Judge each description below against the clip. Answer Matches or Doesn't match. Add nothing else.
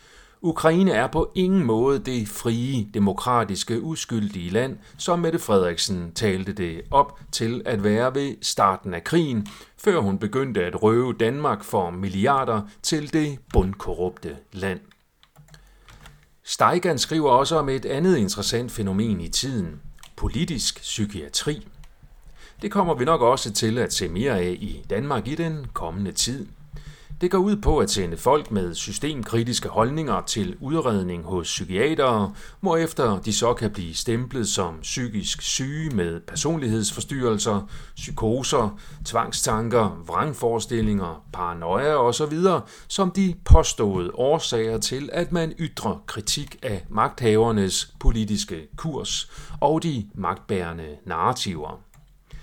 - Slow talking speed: Matches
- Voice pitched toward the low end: Matches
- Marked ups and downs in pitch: Matches